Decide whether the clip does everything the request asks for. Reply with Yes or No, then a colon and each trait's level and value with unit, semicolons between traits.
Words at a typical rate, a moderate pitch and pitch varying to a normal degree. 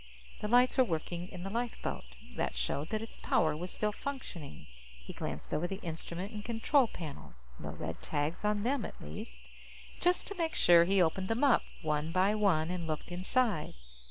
No: average, 185 wpm; medium, 180 Hz; wide, 6.2 semitones